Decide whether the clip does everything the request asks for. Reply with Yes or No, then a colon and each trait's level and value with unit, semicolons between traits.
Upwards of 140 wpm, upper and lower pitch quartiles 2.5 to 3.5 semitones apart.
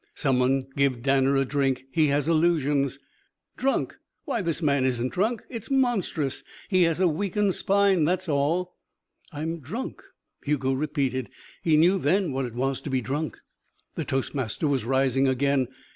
No: average, 160 wpm; average, 4.7 semitones